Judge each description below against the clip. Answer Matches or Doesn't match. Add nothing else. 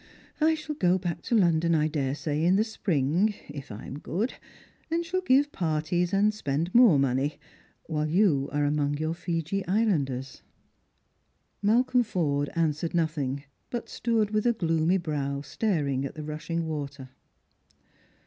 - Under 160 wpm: Matches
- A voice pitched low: Doesn't match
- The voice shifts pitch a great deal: Matches